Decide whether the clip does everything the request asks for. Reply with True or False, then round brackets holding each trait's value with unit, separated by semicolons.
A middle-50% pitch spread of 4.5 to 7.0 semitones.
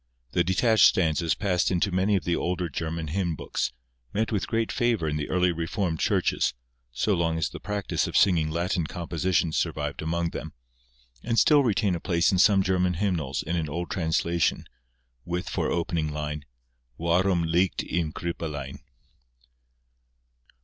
False (2.7 semitones)